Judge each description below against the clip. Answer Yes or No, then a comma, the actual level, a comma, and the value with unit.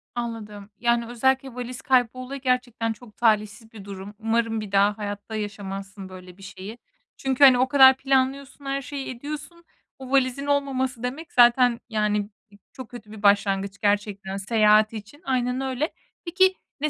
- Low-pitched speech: No, high, 235 Hz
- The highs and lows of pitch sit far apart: No, average, 4.2 semitones